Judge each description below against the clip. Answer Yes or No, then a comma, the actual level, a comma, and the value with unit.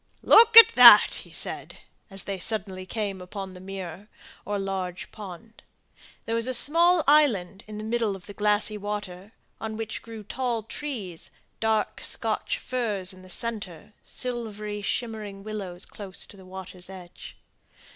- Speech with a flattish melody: No, average, 3.0 semitones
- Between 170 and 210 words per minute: No, average, 155 wpm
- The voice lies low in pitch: No, high, 205 Hz